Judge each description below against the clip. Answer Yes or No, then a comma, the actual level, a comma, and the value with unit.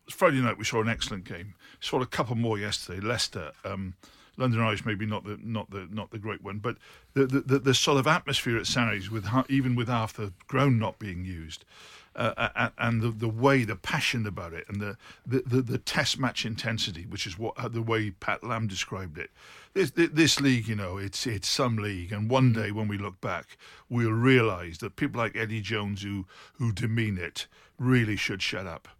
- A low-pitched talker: Yes, low, 115 Hz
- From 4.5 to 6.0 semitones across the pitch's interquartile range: No, average, 3.5 semitones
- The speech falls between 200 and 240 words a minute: Yes, fast, 205 wpm